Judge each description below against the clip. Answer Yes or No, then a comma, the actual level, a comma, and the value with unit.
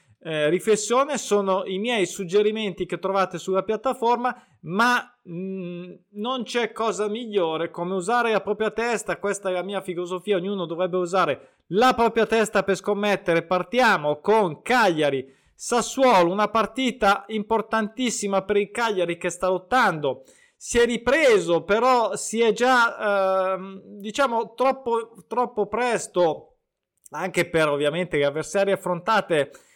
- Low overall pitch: No, high, 205 Hz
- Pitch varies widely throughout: No, average, 4.0 semitones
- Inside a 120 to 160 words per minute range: Yes, average, 130 wpm